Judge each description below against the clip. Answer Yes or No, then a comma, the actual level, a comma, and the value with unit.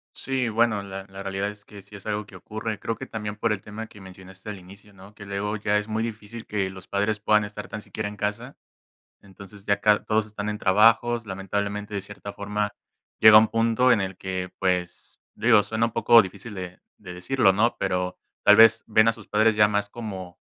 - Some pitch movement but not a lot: No, narrow, 2.0 semitones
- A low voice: Yes, low, 105 Hz